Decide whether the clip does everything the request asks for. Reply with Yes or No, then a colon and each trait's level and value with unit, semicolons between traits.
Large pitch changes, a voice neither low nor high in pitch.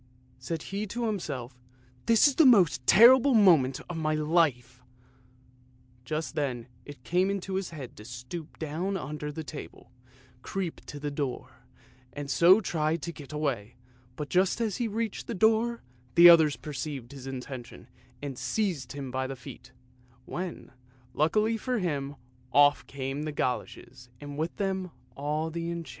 Yes: wide, 5.9 semitones; medium, 155 Hz